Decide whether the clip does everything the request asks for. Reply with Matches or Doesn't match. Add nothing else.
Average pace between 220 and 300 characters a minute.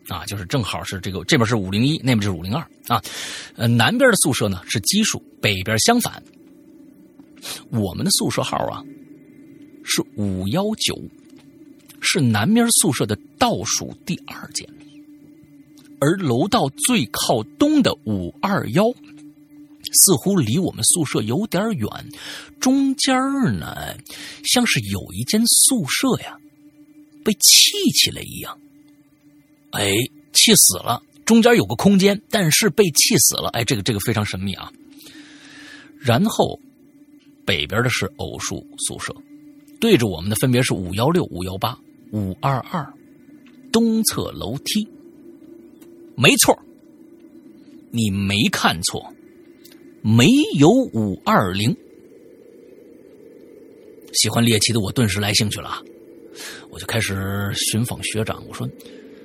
Doesn't match